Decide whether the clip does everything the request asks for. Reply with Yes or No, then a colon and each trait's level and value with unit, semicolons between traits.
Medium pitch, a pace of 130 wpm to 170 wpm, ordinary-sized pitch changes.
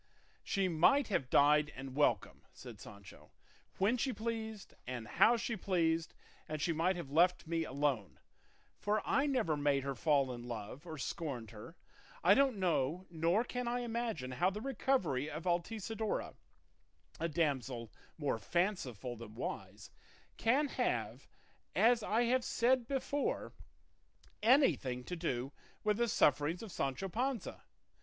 No: medium, 170 Hz; average, 145 wpm; wide, 8.6 semitones